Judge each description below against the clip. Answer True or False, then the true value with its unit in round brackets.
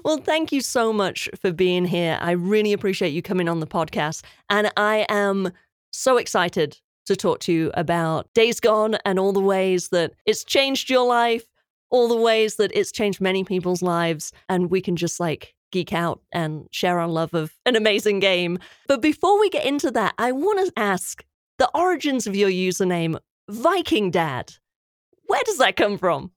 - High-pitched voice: True (200 Hz)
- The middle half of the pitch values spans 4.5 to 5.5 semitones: True (4.8 semitones)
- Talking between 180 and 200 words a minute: True (190 wpm)